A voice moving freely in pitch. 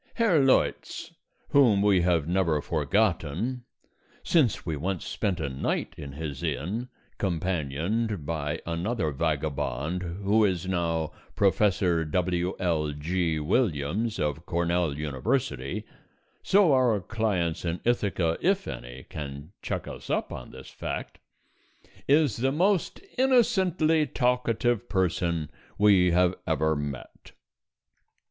Yes: wide, 6.3 semitones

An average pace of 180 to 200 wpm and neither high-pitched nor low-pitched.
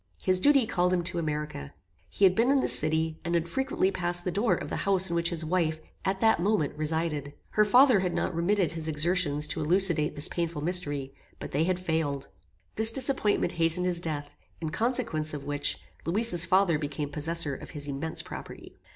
Yes: average, 195 wpm; medium, 170 Hz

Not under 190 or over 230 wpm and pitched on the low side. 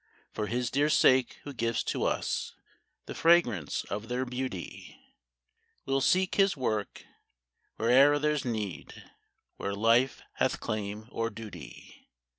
No: slow, 135 wpm; low, 120 Hz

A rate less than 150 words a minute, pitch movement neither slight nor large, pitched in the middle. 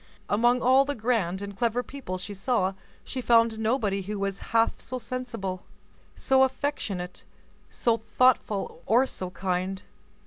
No: average, 140 wpm; average, 4.5 semitones; high, 225 Hz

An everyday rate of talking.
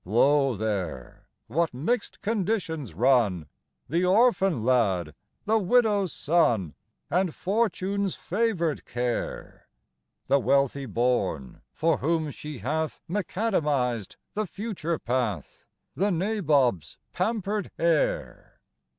No: slow, 105 wpm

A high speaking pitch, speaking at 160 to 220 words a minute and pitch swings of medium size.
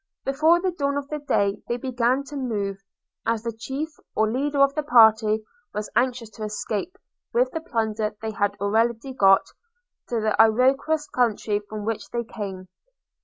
Yes: high, 235 Hz; average, 170 wpm; average, 4.3 semitones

